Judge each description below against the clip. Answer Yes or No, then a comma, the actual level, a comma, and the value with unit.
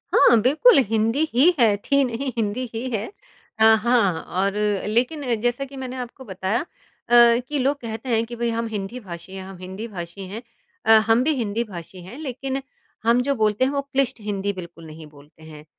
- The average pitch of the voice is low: No, high, 225 Hz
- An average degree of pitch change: Yes, average, 4.4 semitones